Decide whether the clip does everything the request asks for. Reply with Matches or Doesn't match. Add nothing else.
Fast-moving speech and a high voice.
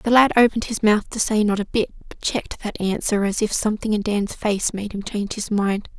Matches